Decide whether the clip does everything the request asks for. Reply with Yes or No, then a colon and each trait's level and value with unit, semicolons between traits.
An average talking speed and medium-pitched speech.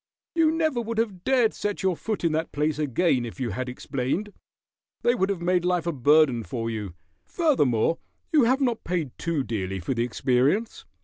Yes: average, 190 wpm; medium, 165 Hz